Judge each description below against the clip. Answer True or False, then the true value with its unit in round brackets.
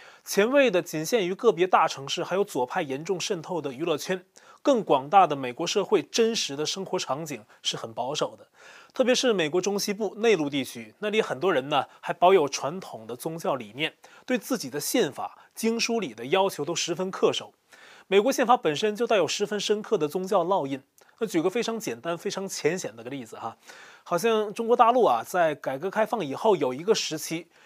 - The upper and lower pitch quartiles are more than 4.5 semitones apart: True (5.2 semitones)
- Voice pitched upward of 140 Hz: True (190 Hz)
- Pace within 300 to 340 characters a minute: True (305 characters per minute)